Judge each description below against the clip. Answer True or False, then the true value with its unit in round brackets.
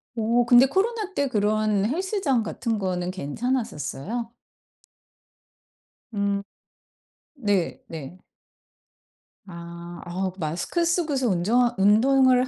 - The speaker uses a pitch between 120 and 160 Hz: False (220 Hz)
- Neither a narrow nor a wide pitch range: False (6.1 semitones)